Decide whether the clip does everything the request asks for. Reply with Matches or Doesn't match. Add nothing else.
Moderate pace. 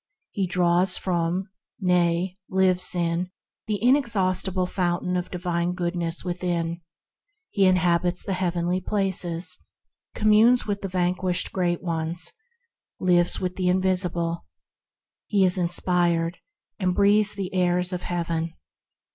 Doesn't match